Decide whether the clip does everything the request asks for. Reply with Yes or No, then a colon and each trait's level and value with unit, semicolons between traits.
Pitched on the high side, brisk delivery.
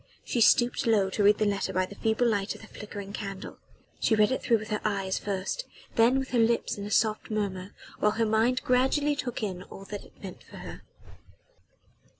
Yes: high, 215 Hz; fast, 210 wpm